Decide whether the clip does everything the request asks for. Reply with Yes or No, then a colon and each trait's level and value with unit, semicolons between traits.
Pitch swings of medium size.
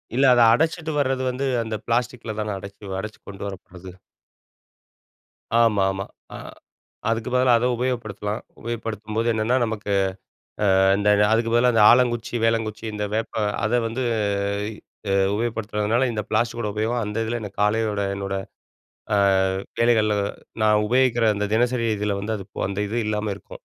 No: narrow, 2.3 semitones